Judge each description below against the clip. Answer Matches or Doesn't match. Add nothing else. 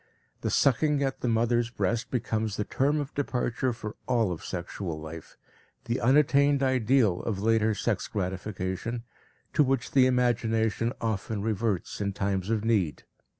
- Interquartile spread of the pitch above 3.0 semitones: Matches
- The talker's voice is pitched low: Matches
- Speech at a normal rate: Matches